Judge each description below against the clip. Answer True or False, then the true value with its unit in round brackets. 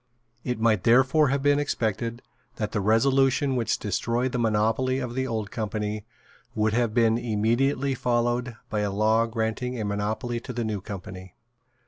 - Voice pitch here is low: True (115 Hz)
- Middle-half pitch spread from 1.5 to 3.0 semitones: True (2.7 semitones)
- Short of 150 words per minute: False (160 wpm)